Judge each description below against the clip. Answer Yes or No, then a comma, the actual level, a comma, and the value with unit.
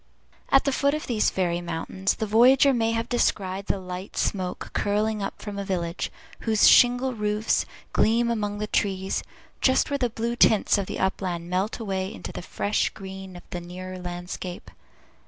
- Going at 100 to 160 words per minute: No, average, 175 wpm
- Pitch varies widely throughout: No, average, 3.6 semitones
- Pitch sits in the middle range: No, high, 205 Hz